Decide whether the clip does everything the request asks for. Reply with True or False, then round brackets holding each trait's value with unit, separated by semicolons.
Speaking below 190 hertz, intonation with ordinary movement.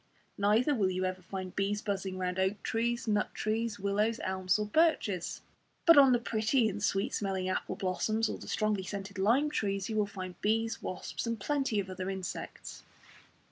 False (205 Hz; 3.0 semitones)